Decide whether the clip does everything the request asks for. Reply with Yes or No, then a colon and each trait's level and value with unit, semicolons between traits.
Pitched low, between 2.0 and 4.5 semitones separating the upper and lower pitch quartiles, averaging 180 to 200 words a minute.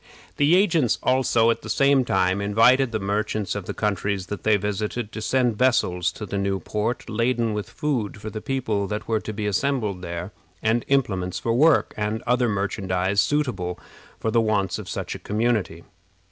Yes: low, 110 Hz; average, 3.4 semitones; average, 185 wpm